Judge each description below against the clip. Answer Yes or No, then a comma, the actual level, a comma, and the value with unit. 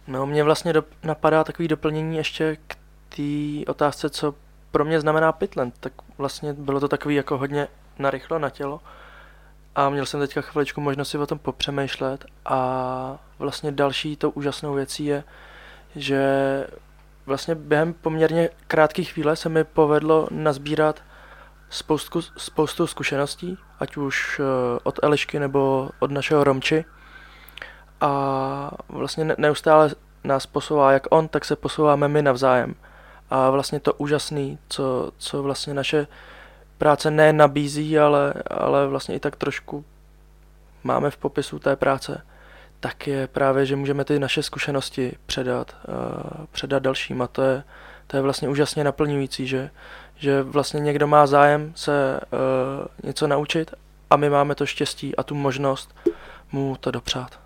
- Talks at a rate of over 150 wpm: No, average, 145 wpm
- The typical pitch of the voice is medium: Yes, medium, 145 Hz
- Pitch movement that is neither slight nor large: No, narrow, 1.9 semitones